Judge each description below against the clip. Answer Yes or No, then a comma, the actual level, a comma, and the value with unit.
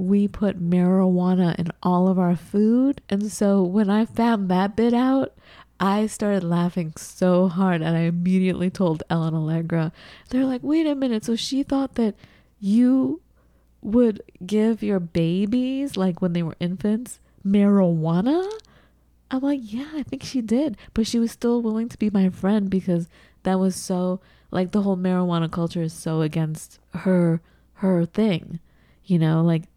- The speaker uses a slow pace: No, average, 165 wpm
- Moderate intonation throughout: Yes, average, 4.6 semitones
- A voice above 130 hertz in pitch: Yes, high, 190 Hz